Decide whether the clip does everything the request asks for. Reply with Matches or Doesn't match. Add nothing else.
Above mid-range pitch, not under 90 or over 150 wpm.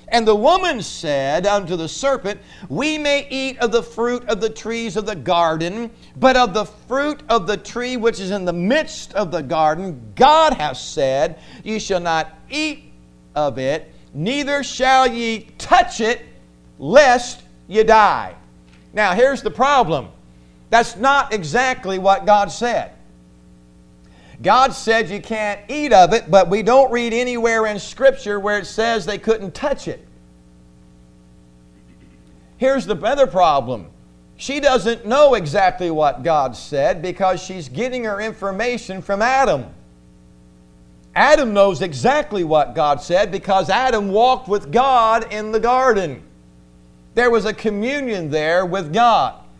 Matches